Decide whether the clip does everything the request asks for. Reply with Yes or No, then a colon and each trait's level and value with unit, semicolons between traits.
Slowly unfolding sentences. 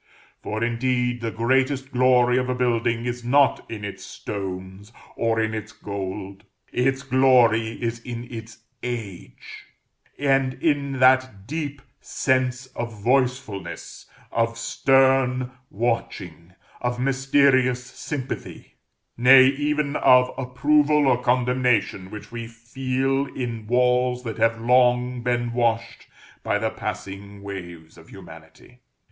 Yes: slow, 120 wpm